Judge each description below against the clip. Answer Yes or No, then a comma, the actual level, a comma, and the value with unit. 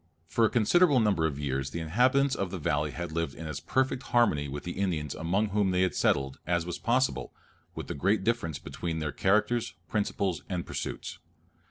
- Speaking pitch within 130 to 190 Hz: No, very low, 90 Hz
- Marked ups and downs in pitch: Yes, wide, 6.0 semitones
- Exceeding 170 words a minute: Yes, average, 195 wpm